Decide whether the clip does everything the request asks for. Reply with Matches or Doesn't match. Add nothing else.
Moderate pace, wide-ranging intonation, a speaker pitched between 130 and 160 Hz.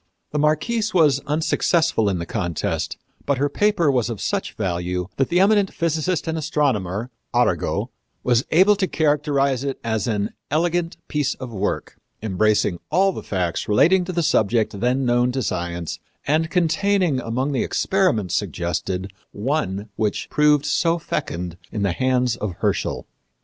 Matches